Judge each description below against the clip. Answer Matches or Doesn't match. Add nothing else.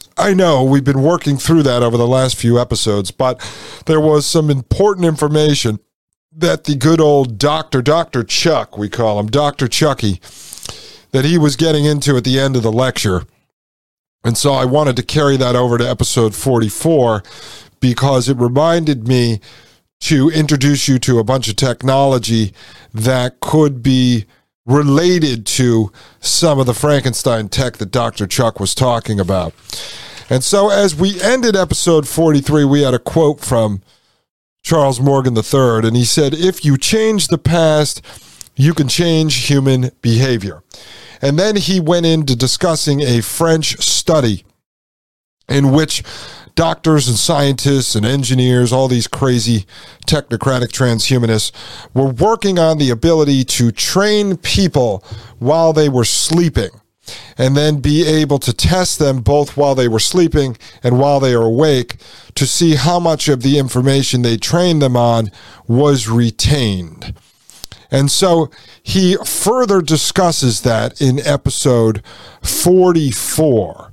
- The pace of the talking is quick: Doesn't match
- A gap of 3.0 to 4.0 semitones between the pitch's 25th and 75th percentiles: Doesn't match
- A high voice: Doesn't match